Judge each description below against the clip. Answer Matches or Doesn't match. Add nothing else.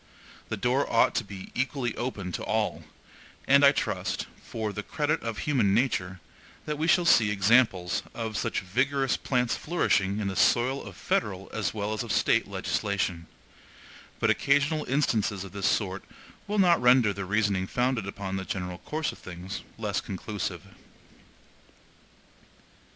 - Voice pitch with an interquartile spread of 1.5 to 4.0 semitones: Doesn't match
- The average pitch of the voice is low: Matches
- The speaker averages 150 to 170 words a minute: Matches